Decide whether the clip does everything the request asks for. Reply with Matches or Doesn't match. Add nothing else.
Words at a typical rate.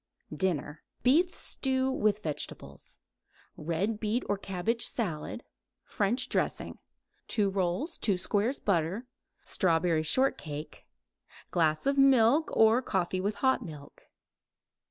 Doesn't match